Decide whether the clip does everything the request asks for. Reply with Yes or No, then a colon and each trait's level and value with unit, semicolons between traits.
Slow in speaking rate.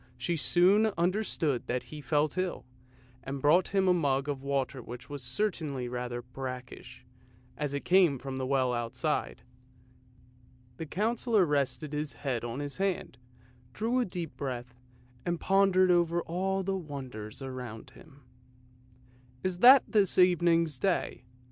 No: average, 145 wpm